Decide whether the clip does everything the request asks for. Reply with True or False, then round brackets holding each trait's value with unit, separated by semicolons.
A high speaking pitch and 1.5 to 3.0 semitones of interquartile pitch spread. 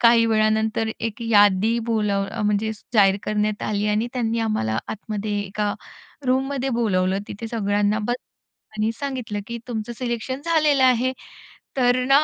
True (220 Hz; 2.7 semitones)